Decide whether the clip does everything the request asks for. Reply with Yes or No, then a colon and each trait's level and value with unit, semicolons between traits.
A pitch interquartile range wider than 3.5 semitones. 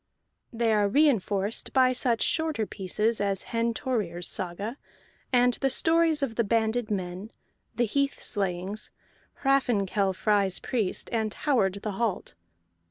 Yes: average, 4.0 semitones